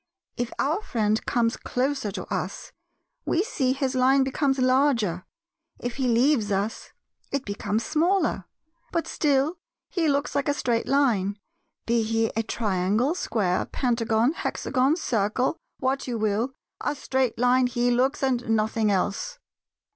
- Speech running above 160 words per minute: No, average, 140 wpm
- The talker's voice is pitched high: Yes, very high, 250 Hz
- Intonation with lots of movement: No, average, 3.8 semitones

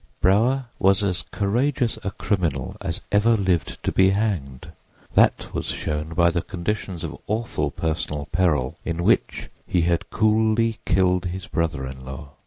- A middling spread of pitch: Yes, average, 4.4 semitones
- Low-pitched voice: Yes, very low, 90 Hz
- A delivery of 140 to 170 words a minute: Yes, average, 155 wpm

